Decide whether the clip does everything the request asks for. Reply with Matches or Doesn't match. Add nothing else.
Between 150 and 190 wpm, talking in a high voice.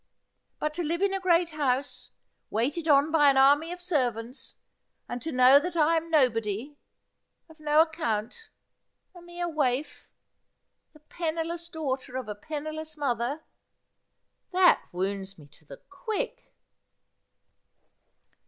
Doesn't match